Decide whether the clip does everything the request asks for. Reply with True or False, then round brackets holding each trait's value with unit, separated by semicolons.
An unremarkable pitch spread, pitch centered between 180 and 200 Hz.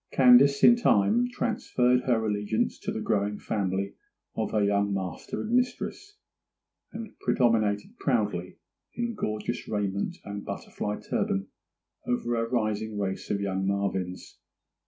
False (4.0 semitones; 105 Hz)